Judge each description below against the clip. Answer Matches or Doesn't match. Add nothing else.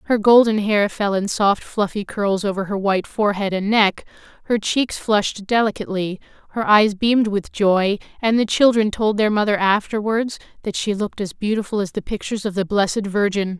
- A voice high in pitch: Matches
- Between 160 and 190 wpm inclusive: Matches